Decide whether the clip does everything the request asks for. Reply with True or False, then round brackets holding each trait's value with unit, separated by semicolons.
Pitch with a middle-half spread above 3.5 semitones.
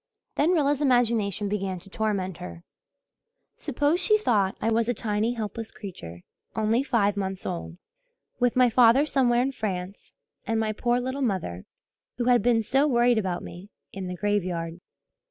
True (4.3 semitones)